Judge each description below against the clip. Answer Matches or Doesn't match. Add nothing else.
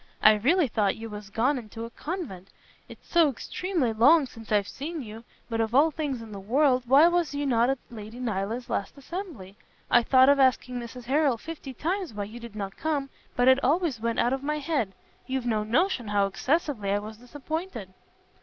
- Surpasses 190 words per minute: Matches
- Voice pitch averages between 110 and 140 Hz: Doesn't match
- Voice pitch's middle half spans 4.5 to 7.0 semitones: Matches